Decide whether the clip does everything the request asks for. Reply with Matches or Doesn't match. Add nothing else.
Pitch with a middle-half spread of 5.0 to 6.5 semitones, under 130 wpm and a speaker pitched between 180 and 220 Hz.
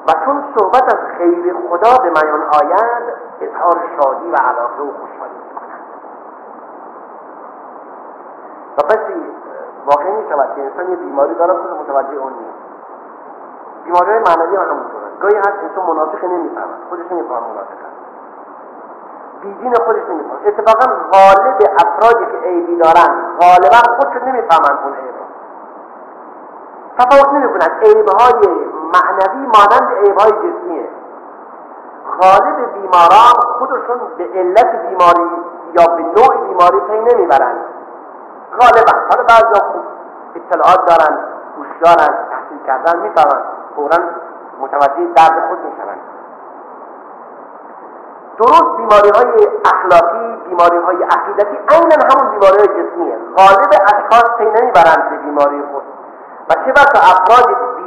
Matches